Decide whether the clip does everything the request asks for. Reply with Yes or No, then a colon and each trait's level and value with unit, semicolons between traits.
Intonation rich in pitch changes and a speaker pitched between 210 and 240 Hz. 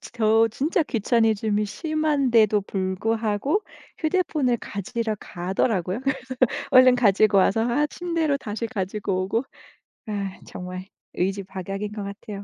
No: average, 4.5 semitones; high, 220 Hz